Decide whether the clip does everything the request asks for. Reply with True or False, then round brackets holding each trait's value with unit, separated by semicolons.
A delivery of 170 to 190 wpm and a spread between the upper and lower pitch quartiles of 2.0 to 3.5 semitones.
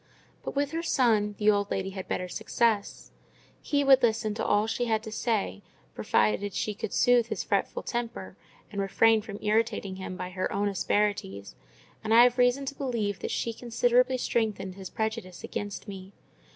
True (180 wpm; 3.1 semitones)